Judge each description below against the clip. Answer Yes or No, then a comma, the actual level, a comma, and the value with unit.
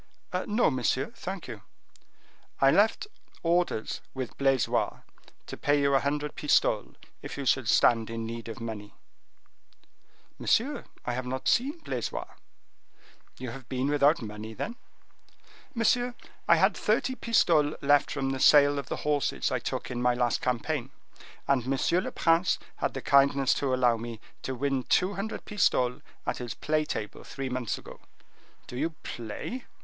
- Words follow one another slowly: No, average, 155 wpm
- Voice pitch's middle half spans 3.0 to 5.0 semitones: Yes, average, 4.4 semitones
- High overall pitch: No, low, 135 Hz